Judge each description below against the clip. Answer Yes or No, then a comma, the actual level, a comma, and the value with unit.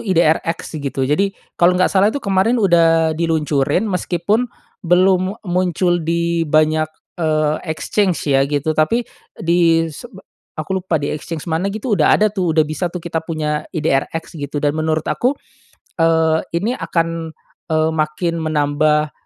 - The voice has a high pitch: No, medium, 165 Hz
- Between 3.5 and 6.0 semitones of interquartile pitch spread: No, average, 2.8 semitones